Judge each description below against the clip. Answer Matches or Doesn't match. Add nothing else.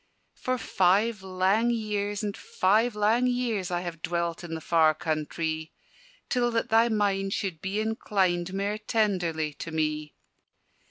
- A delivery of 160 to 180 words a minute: Doesn't match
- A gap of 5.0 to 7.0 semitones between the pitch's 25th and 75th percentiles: Doesn't match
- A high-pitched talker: Matches